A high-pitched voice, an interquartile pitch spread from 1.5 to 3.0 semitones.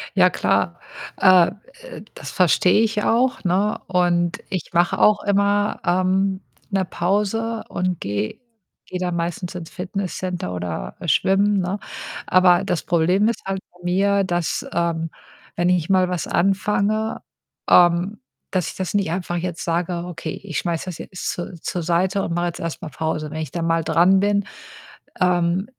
No: medium, 180 Hz; narrow, 2.4 semitones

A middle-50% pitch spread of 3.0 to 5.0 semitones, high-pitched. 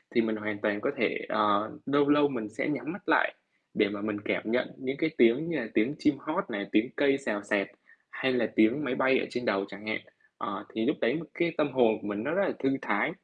No: average, 4.6 semitones; low, 115 Hz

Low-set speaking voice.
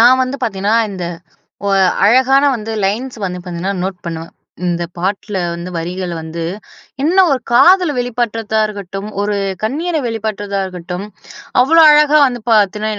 No: high, 210 Hz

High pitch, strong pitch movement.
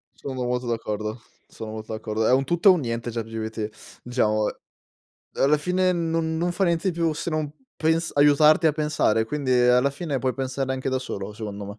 No: low, 130 Hz; wide, 5.9 semitones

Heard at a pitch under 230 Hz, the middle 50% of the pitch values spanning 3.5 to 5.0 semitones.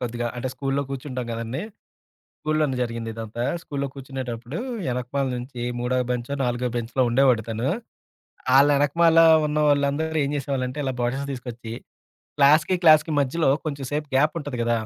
No: low, 135 Hz; average, 2.9 semitones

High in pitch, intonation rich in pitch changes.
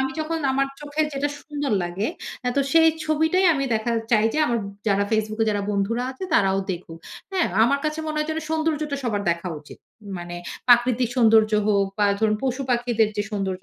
Yes: high, 240 Hz; wide, 6.2 semitones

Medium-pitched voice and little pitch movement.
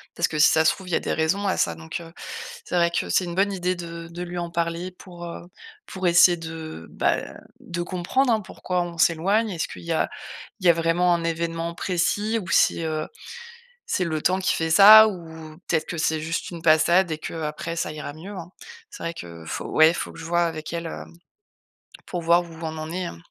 Yes: medium, 170 Hz; narrow, 1.8 semitones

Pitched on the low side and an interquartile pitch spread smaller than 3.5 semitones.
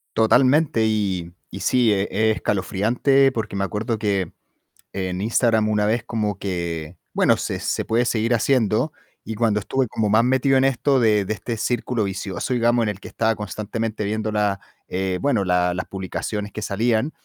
Yes: low, 110 Hz; average, 3.0 semitones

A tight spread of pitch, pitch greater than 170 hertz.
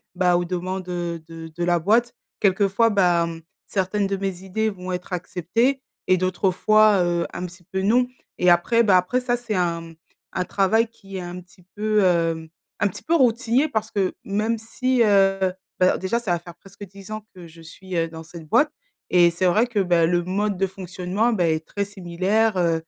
No: average, 3.5 semitones; high, 190 Hz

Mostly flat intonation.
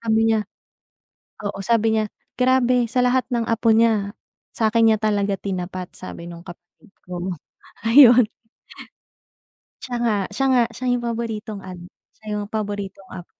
No: average, 3.0 semitones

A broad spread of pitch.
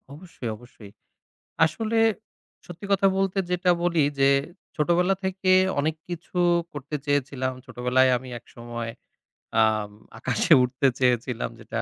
Yes: wide, 6.3 semitones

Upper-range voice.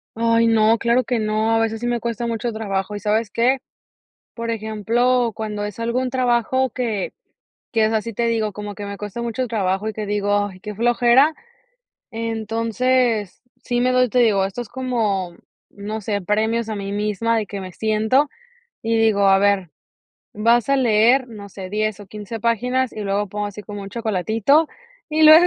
Yes: high, 220 Hz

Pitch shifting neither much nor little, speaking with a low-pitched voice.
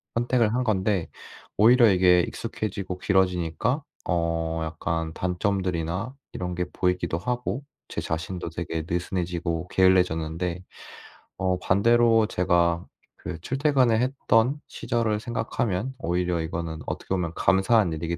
Yes: average, 4.8 semitones; very low, 90 Hz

